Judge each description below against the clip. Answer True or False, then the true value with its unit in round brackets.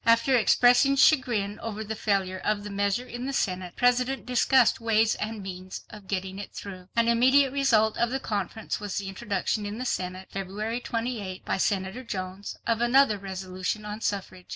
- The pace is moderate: True (180 wpm)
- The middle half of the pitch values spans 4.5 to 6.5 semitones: False (3.8 semitones)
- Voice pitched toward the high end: True (210 Hz)